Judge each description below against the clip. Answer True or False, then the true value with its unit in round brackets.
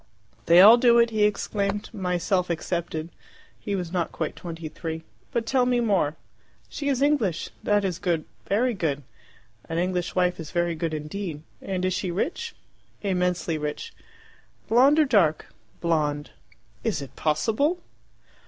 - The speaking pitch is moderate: True (180 Hz)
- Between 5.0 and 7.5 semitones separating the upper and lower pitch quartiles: True (5.3 semitones)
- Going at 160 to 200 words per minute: False (150 wpm)